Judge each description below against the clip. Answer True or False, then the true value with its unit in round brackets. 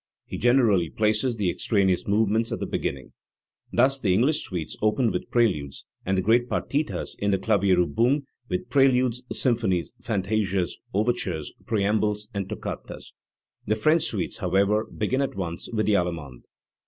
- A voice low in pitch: True (105 Hz)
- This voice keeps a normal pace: True (145 wpm)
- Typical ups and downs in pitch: True (4.2 semitones)